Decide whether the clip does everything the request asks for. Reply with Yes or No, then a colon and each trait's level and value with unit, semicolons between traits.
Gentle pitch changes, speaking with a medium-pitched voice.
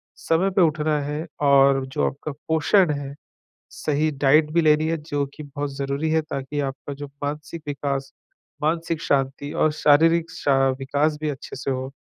Yes: narrow, 2.2 semitones; medium, 150 Hz